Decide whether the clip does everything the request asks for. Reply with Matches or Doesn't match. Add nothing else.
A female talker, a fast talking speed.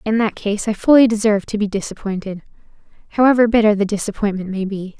Doesn't match